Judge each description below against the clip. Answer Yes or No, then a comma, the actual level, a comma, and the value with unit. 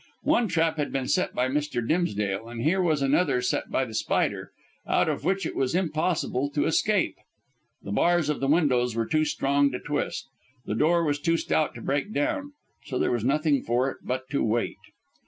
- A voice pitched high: No, medium, 145 Hz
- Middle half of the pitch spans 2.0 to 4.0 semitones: No, average, 4.7 semitones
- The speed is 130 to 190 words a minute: No, average, 200 wpm